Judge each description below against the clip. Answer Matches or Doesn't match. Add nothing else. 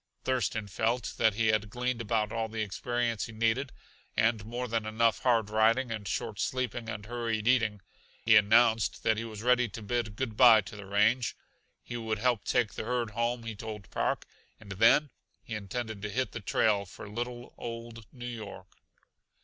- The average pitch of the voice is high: Doesn't match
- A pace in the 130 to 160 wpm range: Doesn't match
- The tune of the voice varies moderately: Doesn't match